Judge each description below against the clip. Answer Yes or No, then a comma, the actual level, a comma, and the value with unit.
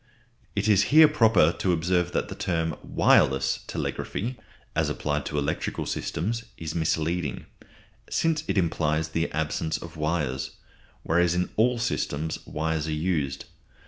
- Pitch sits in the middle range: No, very low, 80 Hz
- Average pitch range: Yes, average, 3.4 semitones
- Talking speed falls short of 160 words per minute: Yes, average, 140 wpm